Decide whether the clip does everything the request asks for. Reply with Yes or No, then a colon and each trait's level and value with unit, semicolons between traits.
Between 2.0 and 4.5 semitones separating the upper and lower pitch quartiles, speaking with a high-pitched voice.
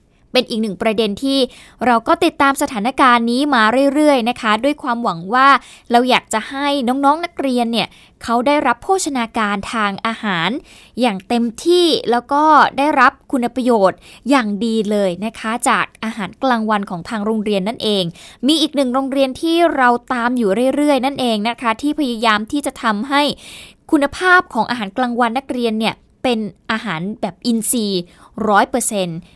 Yes: average, 4.0 semitones; high, 240 Hz